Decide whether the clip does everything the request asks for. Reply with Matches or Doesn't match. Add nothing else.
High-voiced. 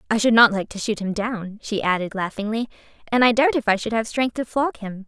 Matches